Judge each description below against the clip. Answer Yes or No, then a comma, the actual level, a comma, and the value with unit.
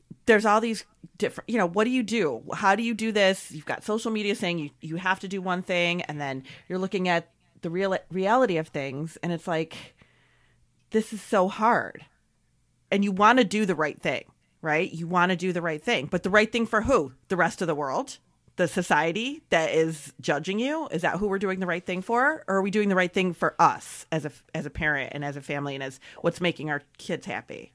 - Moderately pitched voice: Yes, medium, 180 Hz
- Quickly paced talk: Yes, fast, 240 wpm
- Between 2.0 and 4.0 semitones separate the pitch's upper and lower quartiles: No, average, 4.6 semitones